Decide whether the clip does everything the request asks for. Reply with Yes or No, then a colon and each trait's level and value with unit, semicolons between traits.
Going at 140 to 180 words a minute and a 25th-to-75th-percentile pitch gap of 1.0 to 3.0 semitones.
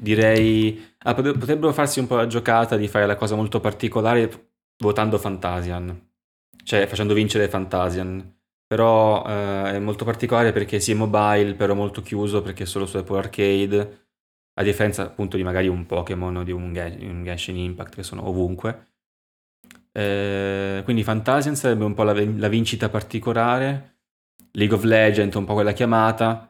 Yes: average, 160 wpm; narrow, 2.4 semitones